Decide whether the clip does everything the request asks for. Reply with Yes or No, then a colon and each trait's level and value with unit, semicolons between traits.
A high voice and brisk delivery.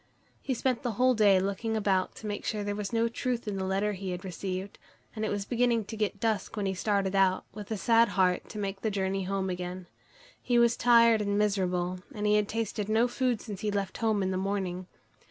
Yes: high, 205 Hz; fast, 230 wpm